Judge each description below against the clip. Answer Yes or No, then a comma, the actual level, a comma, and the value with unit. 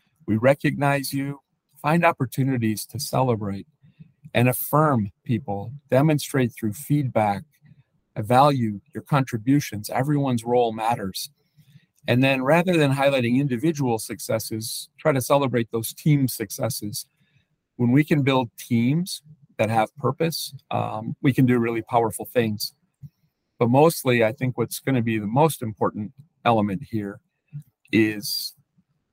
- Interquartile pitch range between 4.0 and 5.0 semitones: Yes, average, 4.6 semitones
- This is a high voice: No, low, 135 Hz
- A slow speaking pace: Yes, slow, 125 wpm